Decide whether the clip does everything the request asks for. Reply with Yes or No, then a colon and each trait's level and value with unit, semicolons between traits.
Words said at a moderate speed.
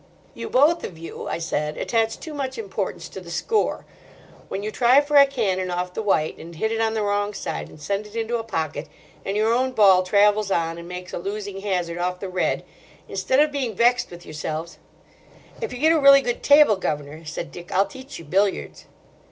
No: fast, 215 wpm